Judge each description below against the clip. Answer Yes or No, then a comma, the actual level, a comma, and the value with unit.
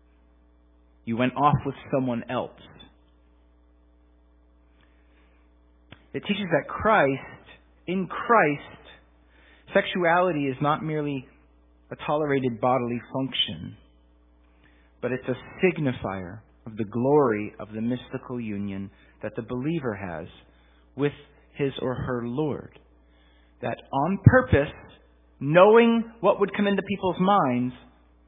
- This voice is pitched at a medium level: No, low, 120 Hz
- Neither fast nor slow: No, slow, 105 wpm